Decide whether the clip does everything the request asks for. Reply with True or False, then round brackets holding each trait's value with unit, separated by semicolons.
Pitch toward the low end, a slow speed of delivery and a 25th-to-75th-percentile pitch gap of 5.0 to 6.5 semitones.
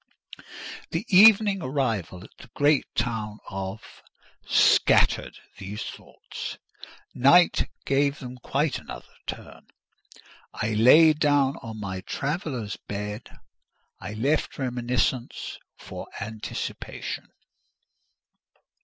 True (125 Hz; 90 wpm; 5.3 semitones)